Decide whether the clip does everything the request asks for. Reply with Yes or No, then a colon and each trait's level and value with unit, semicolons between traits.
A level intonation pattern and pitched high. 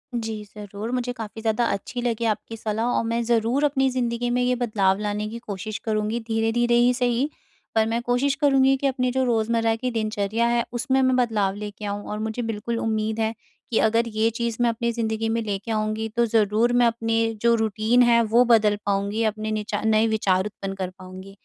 Yes: narrow, 1.9 semitones; high, 225 Hz